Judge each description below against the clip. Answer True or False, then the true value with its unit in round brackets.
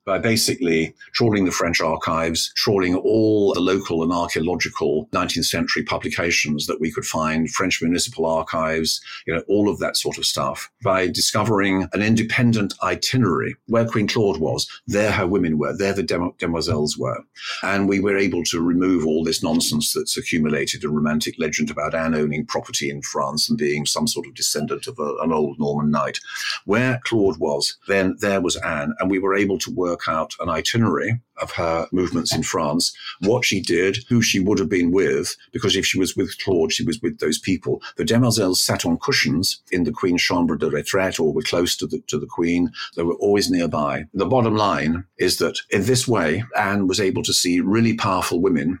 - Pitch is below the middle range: True (95 Hz)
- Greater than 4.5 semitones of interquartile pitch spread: True (5.1 semitones)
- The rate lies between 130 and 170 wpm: False (195 wpm)